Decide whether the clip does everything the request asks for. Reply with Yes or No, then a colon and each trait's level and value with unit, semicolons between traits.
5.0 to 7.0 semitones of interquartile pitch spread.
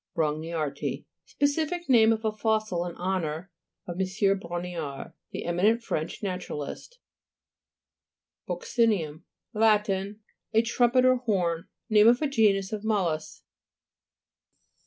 No: average, 4.6 semitones